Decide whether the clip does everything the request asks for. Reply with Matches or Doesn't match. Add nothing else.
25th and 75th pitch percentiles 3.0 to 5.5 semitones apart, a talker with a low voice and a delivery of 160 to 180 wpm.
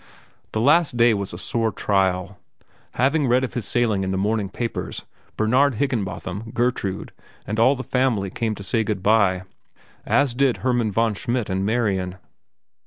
Matches